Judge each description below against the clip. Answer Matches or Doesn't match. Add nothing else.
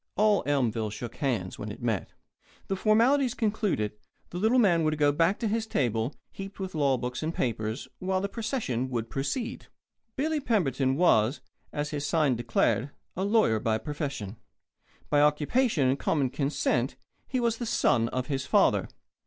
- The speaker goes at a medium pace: Matches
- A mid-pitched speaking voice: Matches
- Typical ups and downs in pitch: Doesn't match